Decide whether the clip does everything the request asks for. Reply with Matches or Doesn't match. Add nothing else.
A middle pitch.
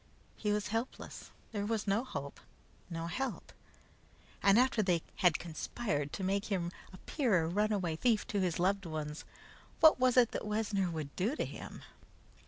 Doesn't match